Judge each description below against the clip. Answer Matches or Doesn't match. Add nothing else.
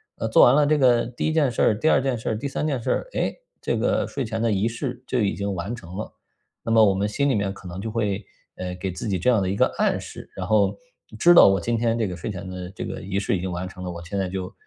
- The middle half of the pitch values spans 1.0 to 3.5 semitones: Doesn't match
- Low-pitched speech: Matches